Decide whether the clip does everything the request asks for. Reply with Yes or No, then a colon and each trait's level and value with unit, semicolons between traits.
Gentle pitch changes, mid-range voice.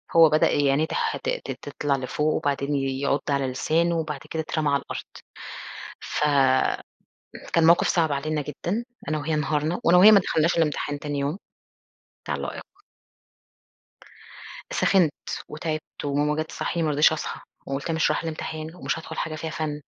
Yes: narrow, 2.1 semitones; medium, 155 Hz